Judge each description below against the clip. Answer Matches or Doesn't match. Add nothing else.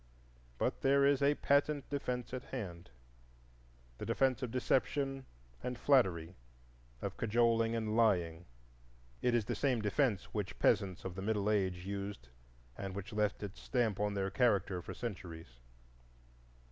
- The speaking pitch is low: Matches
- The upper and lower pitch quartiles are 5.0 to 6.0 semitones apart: Matches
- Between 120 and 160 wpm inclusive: Matches